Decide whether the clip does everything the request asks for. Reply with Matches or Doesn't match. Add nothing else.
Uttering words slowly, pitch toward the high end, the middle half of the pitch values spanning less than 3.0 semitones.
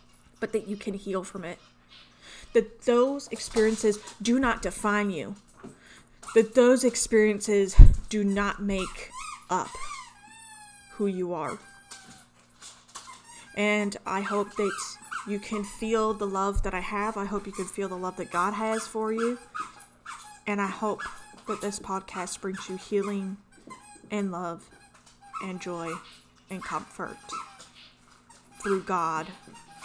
Matches